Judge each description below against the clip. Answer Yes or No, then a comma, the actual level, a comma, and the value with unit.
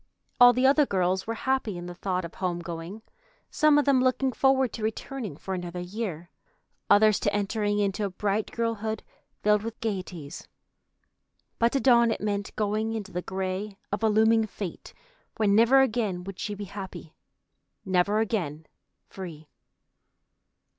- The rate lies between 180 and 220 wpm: No, average, 160 wpm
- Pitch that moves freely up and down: No, average, 3.5 semitones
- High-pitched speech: Yes, high, 205 Hz